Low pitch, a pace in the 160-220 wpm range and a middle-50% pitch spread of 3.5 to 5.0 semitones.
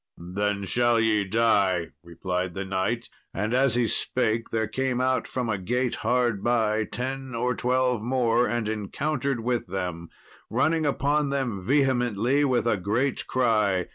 No: low, 115 Hz; average, 150 wpm; average, 4.0 semitones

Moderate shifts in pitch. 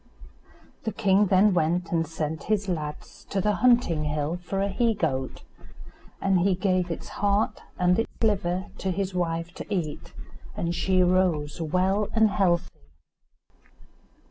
Yes: average, 3.1 semitones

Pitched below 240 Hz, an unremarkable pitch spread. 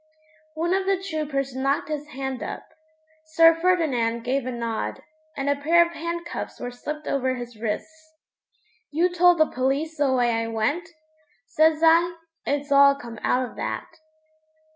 No: very high, 285 Hz; average, 4.5 semitones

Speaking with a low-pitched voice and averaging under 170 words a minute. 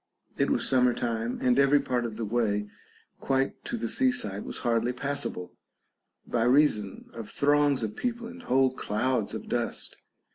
Yes: low, 125 Hz; average, 160 wpm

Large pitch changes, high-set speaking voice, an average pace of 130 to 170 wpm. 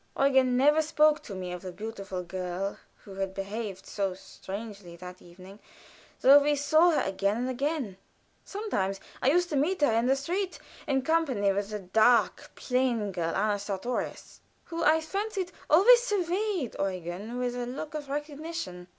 Yes: wide, 7.7 semitones; high, 245 Hz; average, 165 wpm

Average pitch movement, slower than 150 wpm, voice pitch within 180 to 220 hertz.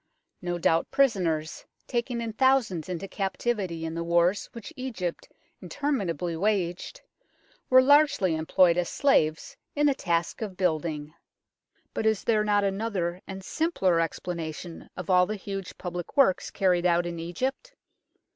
Yes: average, 4.7 semitones; average, 140 wpm; medium, 185 Hz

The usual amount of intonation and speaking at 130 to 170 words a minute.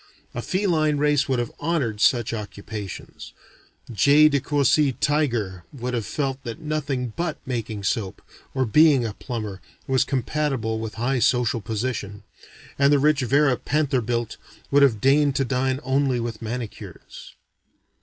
Yes: average, 4.0 semitones; average, 145 wpm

